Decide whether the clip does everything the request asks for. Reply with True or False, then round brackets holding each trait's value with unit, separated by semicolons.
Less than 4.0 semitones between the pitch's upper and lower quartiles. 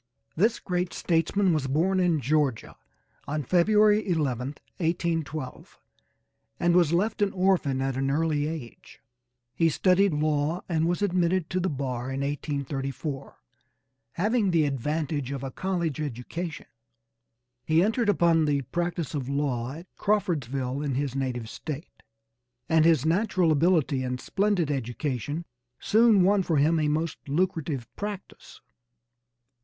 False (4.4 semitones)